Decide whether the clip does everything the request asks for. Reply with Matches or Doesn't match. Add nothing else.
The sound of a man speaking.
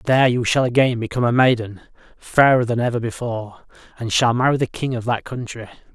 Matches